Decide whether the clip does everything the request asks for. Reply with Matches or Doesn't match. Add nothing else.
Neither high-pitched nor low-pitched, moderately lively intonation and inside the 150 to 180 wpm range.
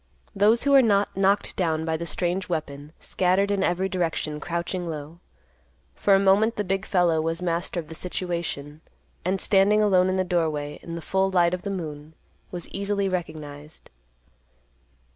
Matches